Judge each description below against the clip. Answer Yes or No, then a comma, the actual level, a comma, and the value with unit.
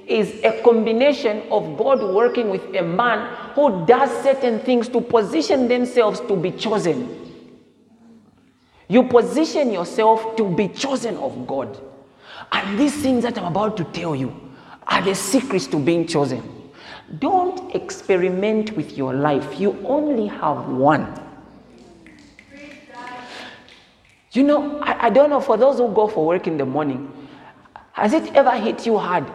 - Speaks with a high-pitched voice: Yes, high, 225 Hz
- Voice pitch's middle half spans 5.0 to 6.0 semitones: Yes, average, 5.3 semitones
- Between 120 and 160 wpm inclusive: Yes, average, 145 wpm